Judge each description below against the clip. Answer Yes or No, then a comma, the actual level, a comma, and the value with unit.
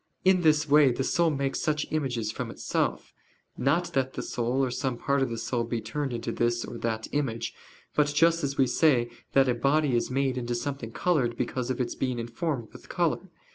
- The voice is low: Yes, low, 130 Hz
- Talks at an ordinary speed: No, fast, 210 wpm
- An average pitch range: Yes, average, 3.7 semitones